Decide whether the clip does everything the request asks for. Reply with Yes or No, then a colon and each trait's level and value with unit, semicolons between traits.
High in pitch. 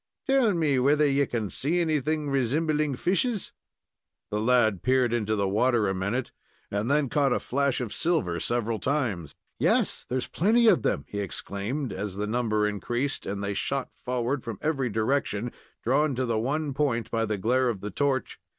No: low, 125 Hz